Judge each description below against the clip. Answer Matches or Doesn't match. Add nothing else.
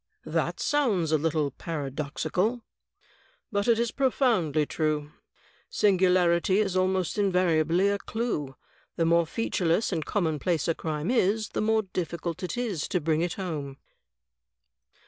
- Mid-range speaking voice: Matches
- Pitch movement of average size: Matches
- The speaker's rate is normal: Doesn't match